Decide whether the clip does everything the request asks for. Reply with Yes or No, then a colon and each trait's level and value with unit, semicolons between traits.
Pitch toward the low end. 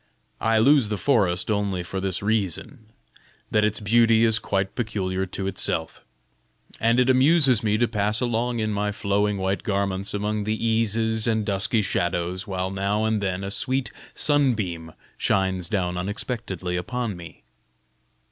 Yes: low, 105 Hz